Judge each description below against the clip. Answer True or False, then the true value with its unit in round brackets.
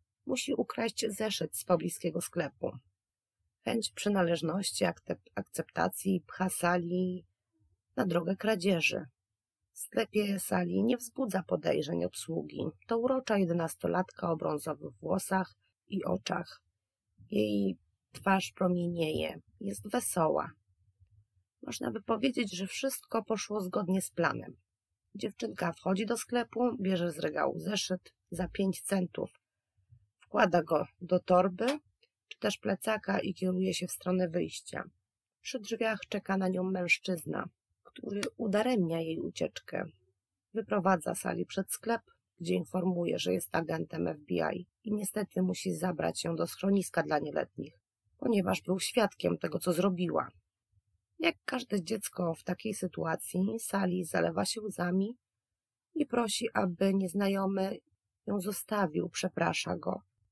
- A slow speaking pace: False (120 wpm)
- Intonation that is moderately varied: False (6.3 semitones)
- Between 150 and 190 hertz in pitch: True (185 Hz)